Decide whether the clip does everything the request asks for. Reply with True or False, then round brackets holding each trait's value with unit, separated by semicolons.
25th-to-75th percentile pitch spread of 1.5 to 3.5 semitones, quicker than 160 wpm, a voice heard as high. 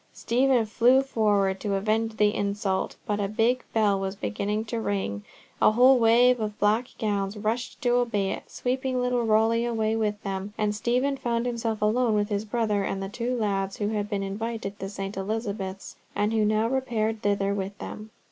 True (2.6 semitones; 190 wpm; 215 Hz)